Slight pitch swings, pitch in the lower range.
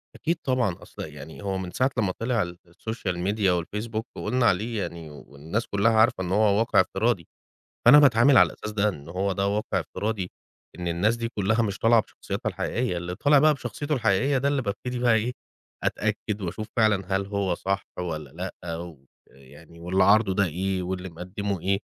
No: average, 4.3 semitones; low, 100 Hz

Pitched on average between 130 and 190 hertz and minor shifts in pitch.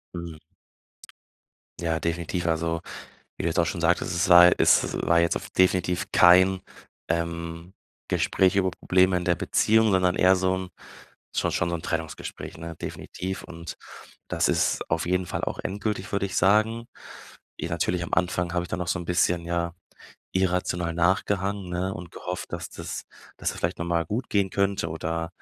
No: very low, 90 Hz; narrow, 1.8 semitones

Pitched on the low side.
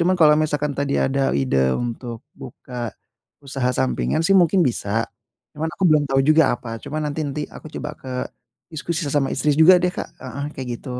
No: medium, 145 Hz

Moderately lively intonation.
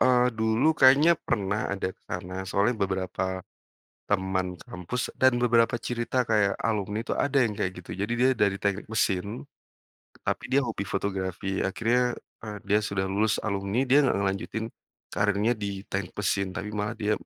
Yes: average, 3.5 semitones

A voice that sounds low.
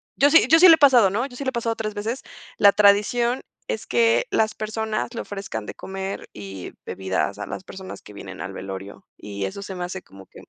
No: high, 200 Hz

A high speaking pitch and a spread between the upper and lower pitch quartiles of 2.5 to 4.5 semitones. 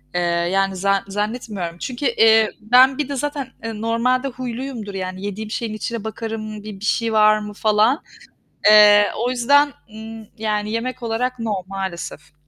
Yes: high, 220 Hz; average, 2.8 semitones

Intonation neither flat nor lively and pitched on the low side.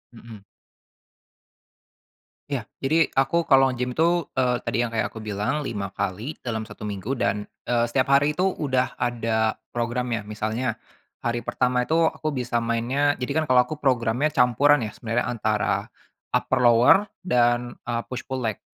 Yes: average, 3.1 semitones; low, 120 Hz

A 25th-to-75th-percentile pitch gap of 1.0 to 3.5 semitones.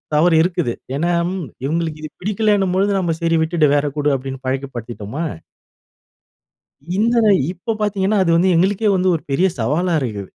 No: average, 4.9 semitones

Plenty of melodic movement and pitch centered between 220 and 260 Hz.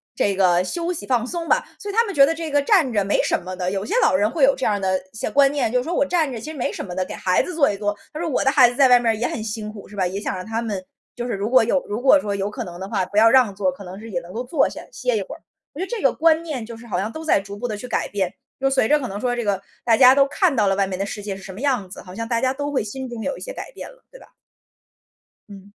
Yes: wide, 5.7 semitones; high, 230 Hz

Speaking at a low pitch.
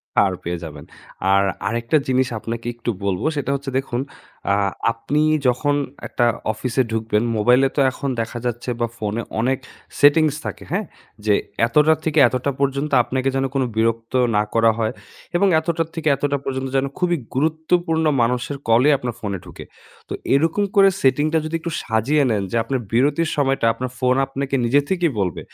Yes: low, 130 Hz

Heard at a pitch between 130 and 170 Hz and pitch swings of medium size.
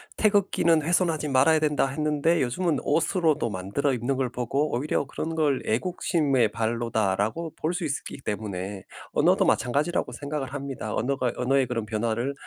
Yes: medium, 140 Hz; average, 4.9 semitones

